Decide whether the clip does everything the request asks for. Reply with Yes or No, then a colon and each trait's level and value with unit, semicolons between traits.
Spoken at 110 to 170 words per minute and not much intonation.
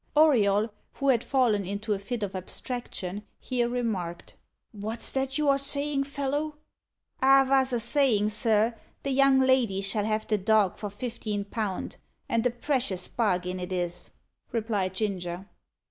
No: average, 150 wpm; average, 4.9 semitones